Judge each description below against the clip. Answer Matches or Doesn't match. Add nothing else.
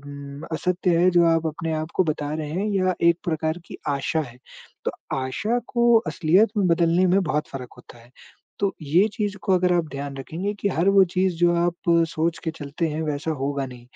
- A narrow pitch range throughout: Doesn't match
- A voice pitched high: Doesn't match